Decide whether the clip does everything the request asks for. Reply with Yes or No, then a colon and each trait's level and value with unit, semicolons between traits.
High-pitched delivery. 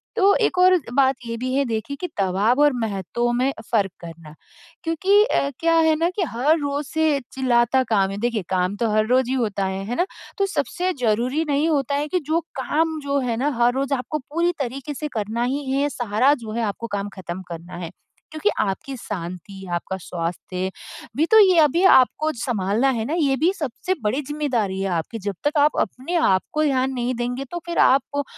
Yes: very high, 260 Hz